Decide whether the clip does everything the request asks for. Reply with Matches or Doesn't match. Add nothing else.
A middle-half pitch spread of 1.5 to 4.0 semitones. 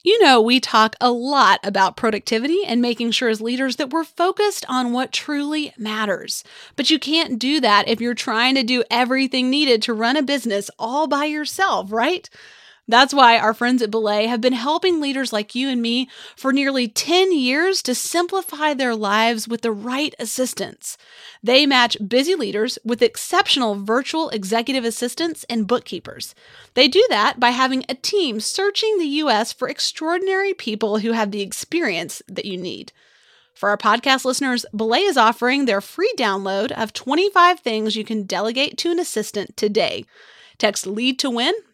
Doesn't match